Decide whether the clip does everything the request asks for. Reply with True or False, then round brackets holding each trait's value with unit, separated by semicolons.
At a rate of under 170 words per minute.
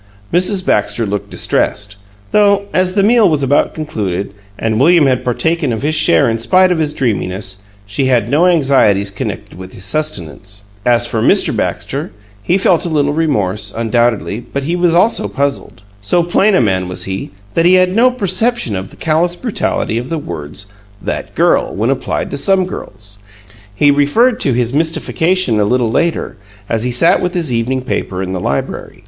False (185 wpm)